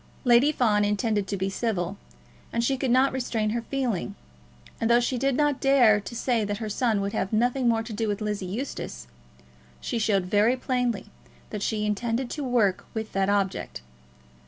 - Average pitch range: Yes, average, 3.3 semitones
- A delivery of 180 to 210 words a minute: Yes, average, 185 wpm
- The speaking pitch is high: Yes, high, 225 Hz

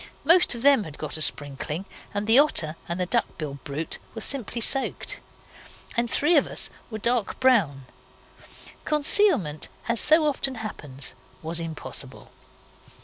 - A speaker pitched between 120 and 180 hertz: No, high, 220 Hz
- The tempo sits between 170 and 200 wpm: No, average, 145 wpm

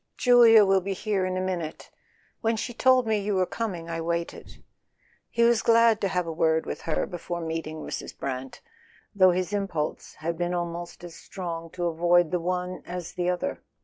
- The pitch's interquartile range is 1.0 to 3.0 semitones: No, average, 3.4 semitones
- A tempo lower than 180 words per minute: No, average, 190 wpm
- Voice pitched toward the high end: No, medium, 180 Hz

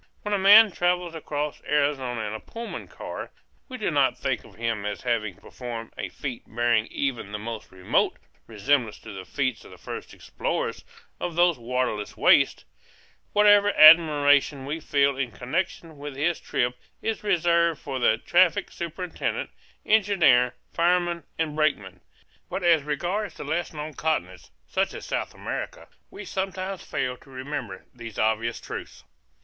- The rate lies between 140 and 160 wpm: Yes, average, 155 wpm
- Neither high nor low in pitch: Yes, medium, 145 Hz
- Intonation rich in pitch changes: Yes, wide, 6.4 semitones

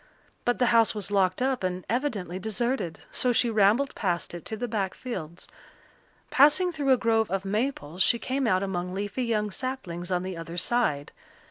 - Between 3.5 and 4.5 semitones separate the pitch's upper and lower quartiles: No, average, 5.1 semitones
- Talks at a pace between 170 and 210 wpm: Yes, average, 185 wpm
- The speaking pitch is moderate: No, high, 210 Hz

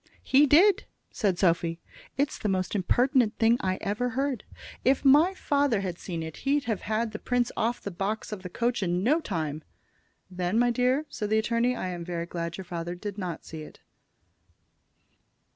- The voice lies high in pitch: Yes, high, 210 Hz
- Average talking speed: Yes, average, 190 wpm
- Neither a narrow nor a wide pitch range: No, wide, 5.8 semitones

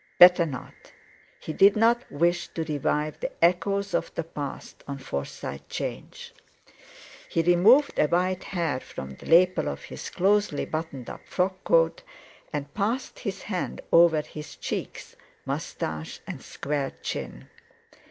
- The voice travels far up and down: No, average, 4.8 semitones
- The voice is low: No, medium, 170 Hz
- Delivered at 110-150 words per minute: Yes, average, 140 wpm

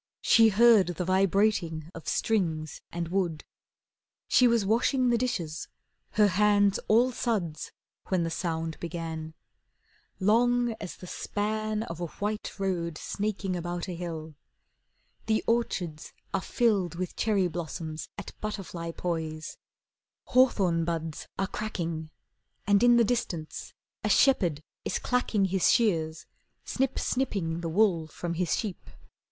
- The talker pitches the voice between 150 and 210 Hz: Yes, medium, 185 Hz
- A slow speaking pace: Yes, slow, 130 wpm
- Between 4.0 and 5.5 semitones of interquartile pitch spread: Yes, average, 4.6 semitones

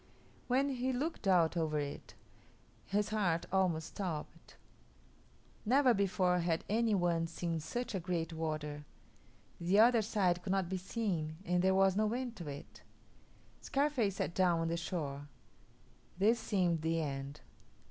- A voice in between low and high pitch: Yes, medium, 180 Hz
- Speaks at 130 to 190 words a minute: Yes, average, 145 wpm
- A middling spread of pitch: Yes, average, 4.5 semitones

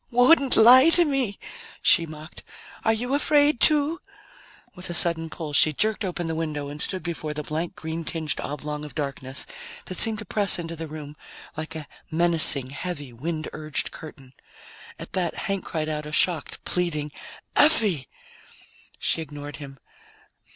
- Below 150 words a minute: No, average, 160 wpm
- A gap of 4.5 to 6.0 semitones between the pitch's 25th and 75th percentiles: Yes, average, 5.2 semitones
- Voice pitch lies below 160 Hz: No, medium, 165 Hz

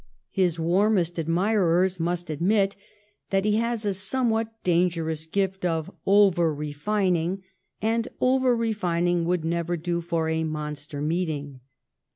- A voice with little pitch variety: No, average, 3.6 semitones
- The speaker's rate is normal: No, slow, 125 wpm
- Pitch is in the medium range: Yes, medium, 175 Hz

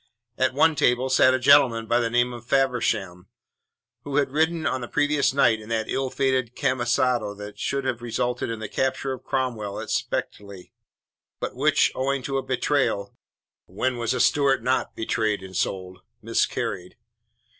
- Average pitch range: Yes, average, 3.2 semitones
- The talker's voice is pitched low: Yes, low, 125 Hz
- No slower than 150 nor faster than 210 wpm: Yes, average, 165 wpm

